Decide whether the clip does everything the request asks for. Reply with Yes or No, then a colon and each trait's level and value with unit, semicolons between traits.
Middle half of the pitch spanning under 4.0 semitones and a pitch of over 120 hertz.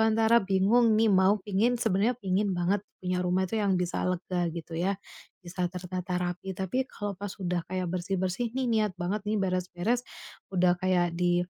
Yes: average, 2.8 semitones; medium, 185 Hz